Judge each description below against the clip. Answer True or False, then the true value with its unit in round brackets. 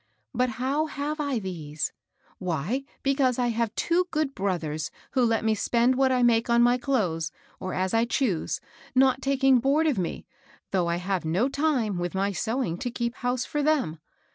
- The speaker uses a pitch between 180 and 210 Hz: False (235 Hz)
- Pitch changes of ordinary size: False (6.2 semitones)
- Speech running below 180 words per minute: False (185 wpm)